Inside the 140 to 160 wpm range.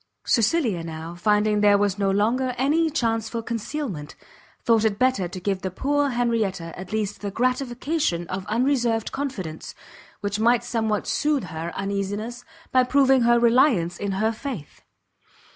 Yes: average, 150 wpm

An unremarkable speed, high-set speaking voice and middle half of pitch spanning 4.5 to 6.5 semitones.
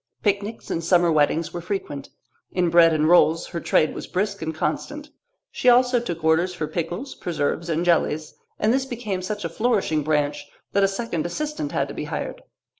No: average, 190 wpm; medium, 175 Hz; average, 4.9 semitones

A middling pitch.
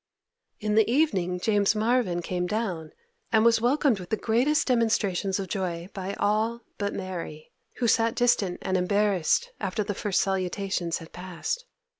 No: high, 200 Hz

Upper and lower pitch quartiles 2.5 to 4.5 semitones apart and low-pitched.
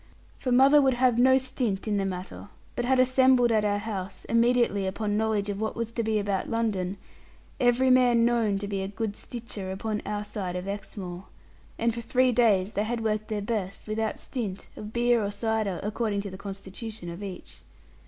No: average, 3.1 semitones; high, 215 Hz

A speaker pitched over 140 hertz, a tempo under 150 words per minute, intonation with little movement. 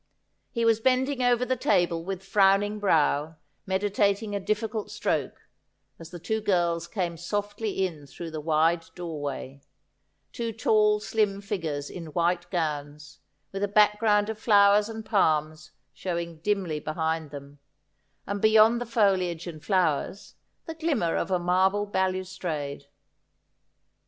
No: high, 190 Hz; average, 140 wpm; average, 4.3 semitones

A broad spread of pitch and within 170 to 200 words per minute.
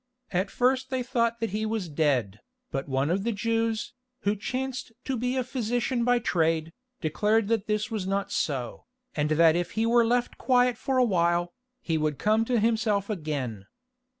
Yes: wide, 6.3 semitones; average, 180 wpm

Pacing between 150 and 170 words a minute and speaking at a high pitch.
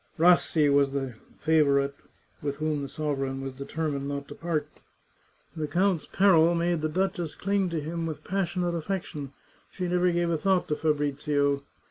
No: average, 160 wpm; medium, 155 Hz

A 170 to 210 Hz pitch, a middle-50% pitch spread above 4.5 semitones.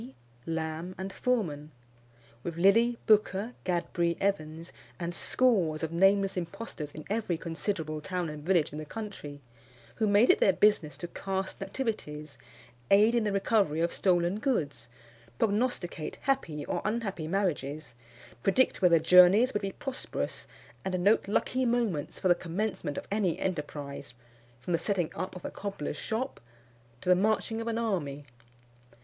Yes: medium, 185 Hz; average, 4.9 semitones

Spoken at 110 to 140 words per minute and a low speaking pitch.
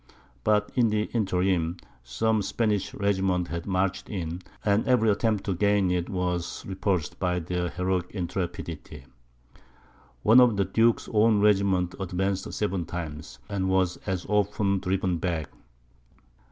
Yes: slow, 135 wpm; very low, 95 Hz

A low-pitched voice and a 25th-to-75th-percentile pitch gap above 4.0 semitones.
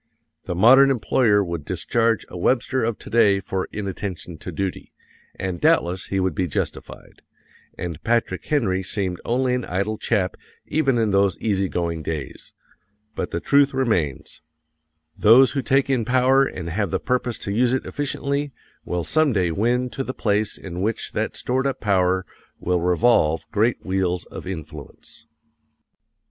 Yes: low, 105 Hz; wide, 5.5 semitones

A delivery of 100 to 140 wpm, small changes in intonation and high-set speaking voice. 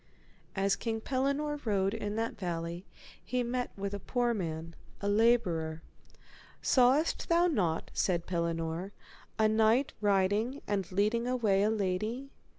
No: slow, 135 wpm; average, 4.7 semitones; high, 205 Hz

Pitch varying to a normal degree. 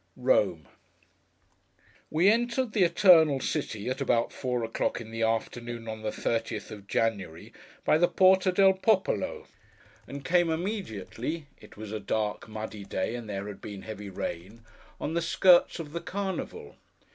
No: wide, 8.5 semitones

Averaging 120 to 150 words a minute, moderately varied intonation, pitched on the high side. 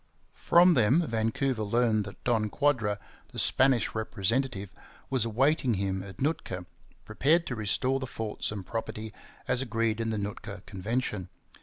No: average, 145 wpm; average, 4.2 semitones; low, 115 Hz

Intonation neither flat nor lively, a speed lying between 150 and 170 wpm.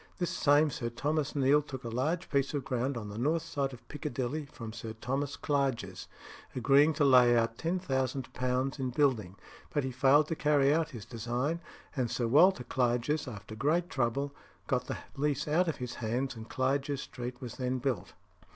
No: average, 3.2 semitones; average, 180 wpm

